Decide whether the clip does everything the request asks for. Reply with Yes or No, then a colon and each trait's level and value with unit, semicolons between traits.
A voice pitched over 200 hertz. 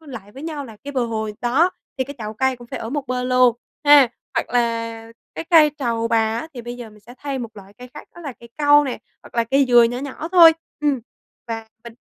Yes: high, 245 Hz